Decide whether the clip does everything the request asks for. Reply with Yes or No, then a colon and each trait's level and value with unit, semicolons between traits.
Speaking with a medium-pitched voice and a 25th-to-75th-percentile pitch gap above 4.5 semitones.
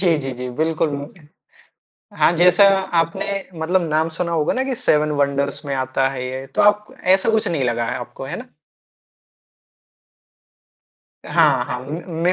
Yes: medium, 155 Hz; average, 4.9 semitones